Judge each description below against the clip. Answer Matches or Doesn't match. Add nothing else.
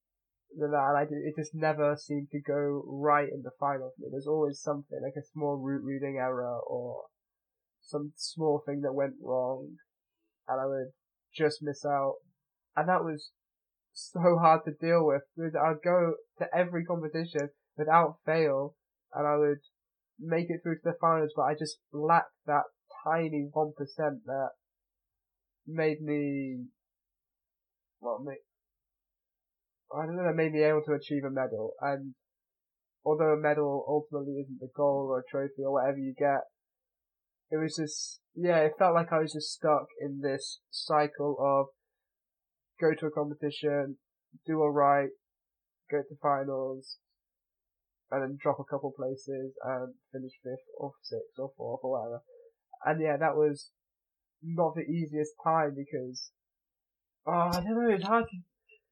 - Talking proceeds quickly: Doesn't match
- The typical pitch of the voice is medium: Matches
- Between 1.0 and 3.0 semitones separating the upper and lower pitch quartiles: Matches